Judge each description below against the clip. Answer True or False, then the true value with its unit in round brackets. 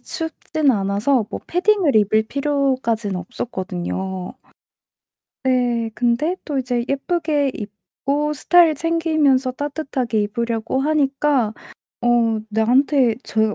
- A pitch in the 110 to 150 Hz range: False (255 Hz)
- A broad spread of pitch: False (4.9 semitones)